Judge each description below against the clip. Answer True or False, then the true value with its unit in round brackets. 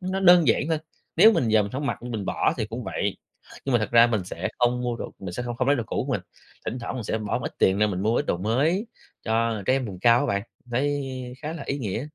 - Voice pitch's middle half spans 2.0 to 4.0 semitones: False (4.4 semitones)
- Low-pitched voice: True (120 Hz)